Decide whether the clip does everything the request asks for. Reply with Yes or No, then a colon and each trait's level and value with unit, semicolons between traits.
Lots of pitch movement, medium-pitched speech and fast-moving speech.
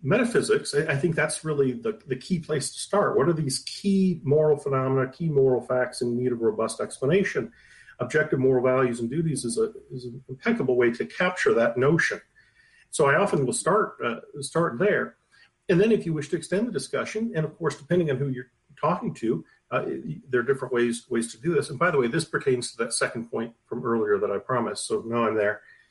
Yes: wide, 6.5 semitones; medium, 150 Hz; fast, 220 wpm